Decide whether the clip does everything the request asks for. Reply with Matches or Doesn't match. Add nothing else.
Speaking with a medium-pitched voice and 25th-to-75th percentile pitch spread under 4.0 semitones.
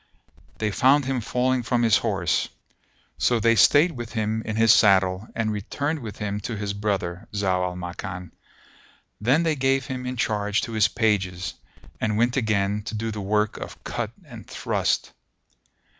Doesn't match